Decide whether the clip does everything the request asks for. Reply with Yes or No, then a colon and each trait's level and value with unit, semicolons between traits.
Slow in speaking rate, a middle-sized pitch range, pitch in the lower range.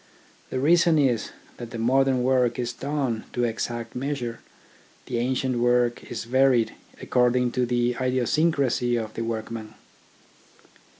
No: slow, 130 wpm; narrow, 1.8 semitones; low, 125 Hz